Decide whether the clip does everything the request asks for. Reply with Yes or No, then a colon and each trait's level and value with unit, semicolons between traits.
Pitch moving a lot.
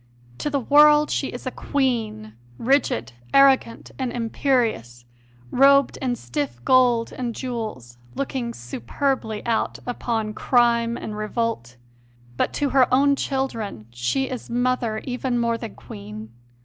No: average, 3.9 semitones